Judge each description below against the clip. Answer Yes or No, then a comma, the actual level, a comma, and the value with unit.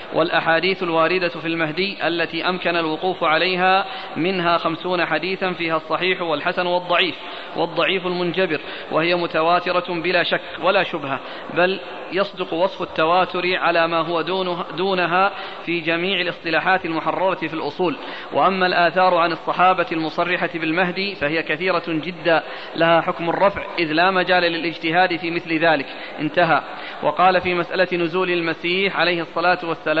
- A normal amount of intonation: No, narrow, 1.8 semitones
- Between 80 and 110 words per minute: No, average, 130 wpm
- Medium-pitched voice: Yes, medium, 175 Hz